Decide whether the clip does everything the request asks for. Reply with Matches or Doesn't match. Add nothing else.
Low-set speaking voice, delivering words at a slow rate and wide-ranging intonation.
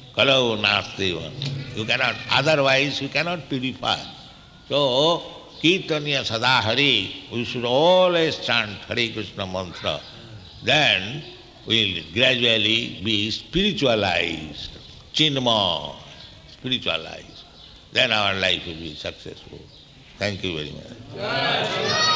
Matches